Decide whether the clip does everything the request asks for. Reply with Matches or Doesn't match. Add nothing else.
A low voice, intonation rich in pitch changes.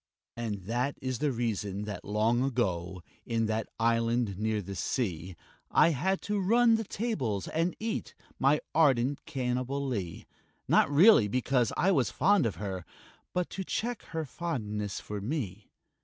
Matches